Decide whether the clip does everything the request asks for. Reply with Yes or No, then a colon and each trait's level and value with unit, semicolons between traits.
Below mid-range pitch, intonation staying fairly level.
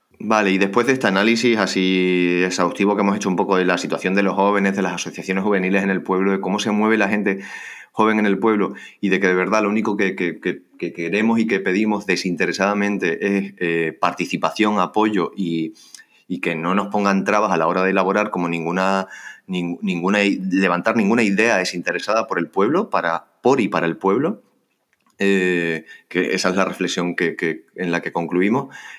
Yes: very low, 95 Hz; narrow, 2.2 semitones